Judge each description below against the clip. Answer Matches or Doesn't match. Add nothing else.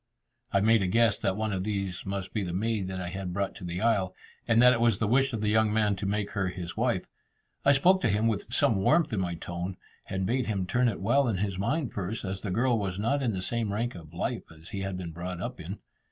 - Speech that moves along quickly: Matches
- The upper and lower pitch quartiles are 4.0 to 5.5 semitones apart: Doesn't match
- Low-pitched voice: Matches